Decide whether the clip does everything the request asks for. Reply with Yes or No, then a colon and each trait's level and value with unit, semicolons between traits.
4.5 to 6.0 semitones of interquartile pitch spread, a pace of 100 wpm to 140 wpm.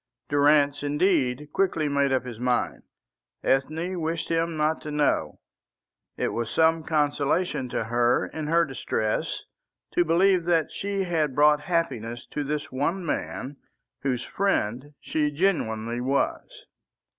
No: average, 4.0 semitones; slow, 135 wpm